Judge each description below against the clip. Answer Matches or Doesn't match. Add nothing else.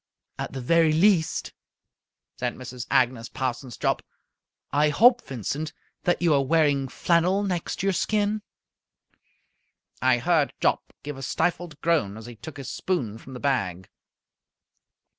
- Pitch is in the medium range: Matches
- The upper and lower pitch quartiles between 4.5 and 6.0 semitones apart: Matches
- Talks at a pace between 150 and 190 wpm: Doesn't match